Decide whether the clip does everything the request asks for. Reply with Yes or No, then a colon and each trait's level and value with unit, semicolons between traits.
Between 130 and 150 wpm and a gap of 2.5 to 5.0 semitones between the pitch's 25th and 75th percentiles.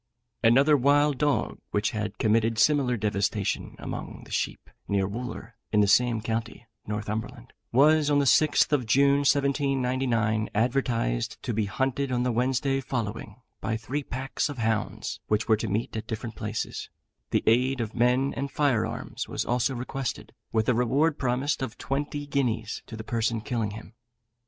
No: average, 165 wpm; average, 3.7 semitones